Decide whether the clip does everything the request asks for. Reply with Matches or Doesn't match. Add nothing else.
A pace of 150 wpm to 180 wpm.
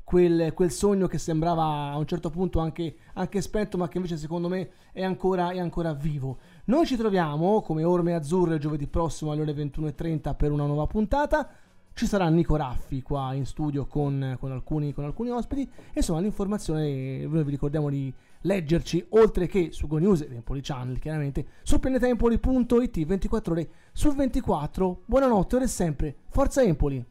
Matches